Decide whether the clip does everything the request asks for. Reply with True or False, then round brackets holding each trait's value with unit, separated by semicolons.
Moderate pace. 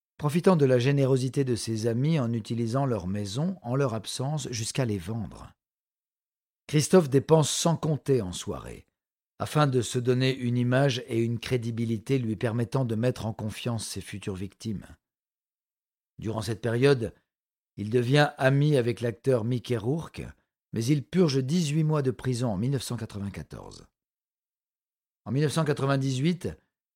False (140 wpm)